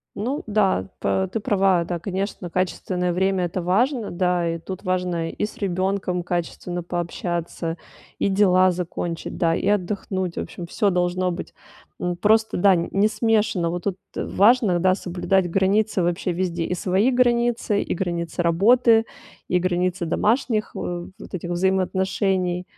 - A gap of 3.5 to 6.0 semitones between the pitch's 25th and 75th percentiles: No, narrow, 2.5 semitones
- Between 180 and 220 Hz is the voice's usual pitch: Yes, medium, 185 Hz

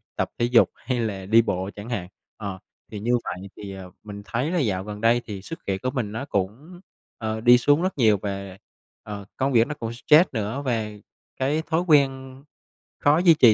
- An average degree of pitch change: Yes, average, 5.0 semitones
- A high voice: No, low, 115 Hz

